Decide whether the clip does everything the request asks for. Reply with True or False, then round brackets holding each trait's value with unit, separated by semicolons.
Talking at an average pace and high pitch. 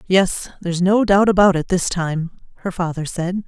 False (190 wpm; 180 Hz)